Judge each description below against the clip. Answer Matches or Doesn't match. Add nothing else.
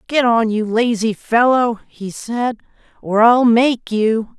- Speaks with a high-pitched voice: Matches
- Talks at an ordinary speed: Matches